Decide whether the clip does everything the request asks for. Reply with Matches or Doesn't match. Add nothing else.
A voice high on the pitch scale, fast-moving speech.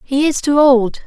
Matches